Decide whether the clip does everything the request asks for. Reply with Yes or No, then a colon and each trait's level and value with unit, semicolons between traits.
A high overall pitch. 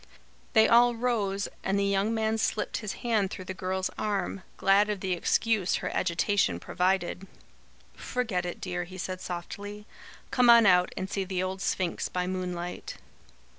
Yes: high, 195 Hz